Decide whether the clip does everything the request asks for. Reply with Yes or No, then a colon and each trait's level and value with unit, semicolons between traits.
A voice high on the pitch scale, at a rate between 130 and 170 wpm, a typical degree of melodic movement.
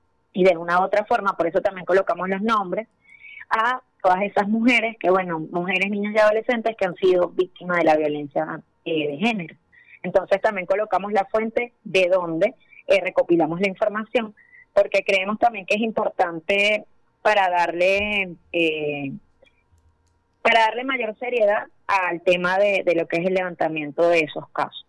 Yes: high, 195 Hz; average, 165 wpm; average, 3.8 semitones